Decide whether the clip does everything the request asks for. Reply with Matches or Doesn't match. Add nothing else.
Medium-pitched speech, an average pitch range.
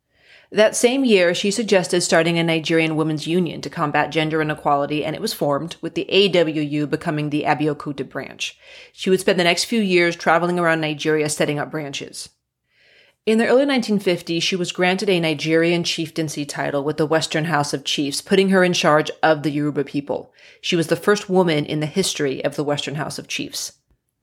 Matches